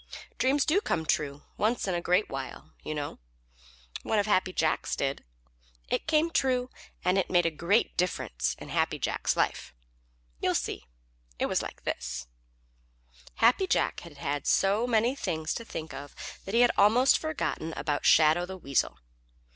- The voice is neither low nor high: Yes, medium, 180 Hz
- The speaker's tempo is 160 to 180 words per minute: Yes, average, 165 wpm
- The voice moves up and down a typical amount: No, wide, 7.5 semitones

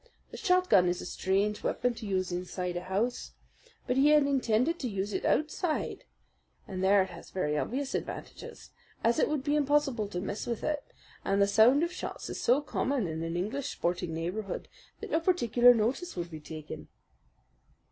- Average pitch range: No, wide, 7.2 semitones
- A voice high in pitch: Yes, high, 220 Hz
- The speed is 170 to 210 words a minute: Yes, average, 185 wpm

